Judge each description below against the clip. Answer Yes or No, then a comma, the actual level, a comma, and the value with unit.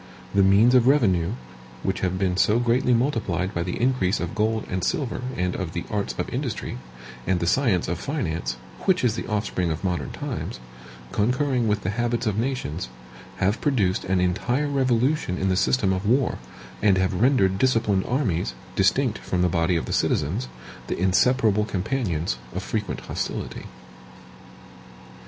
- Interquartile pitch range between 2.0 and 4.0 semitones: No, average, 5.2 semitones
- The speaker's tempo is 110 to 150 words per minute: No, average, 165 wpm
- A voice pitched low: Yes, low, 100 Hz